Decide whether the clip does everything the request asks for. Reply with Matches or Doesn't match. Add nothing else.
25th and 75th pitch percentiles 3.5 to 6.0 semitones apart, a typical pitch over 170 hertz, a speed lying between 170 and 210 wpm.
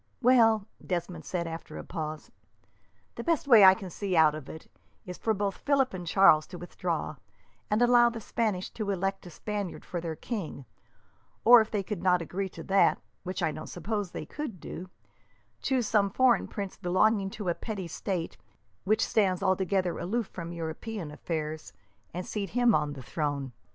Matches